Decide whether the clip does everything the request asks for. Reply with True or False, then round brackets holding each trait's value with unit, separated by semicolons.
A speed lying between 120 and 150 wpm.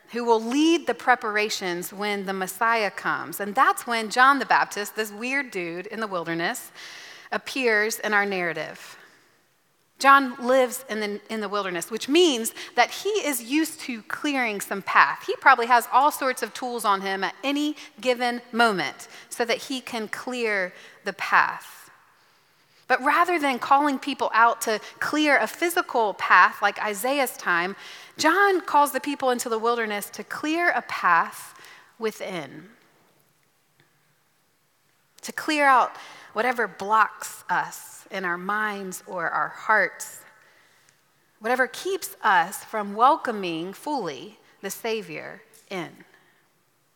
True (140 wpm)